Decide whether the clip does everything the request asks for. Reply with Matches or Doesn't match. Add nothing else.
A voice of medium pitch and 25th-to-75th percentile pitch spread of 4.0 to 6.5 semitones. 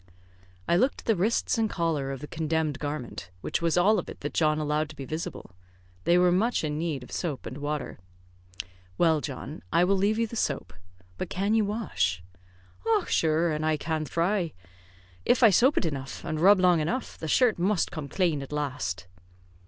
Matches